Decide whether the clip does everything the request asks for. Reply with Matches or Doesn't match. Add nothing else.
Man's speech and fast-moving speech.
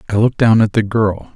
Matches